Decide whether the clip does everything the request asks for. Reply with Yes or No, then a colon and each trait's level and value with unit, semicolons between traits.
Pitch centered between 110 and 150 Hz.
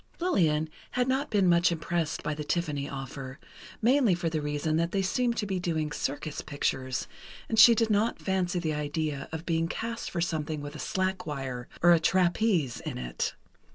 No: medium, 165 Hz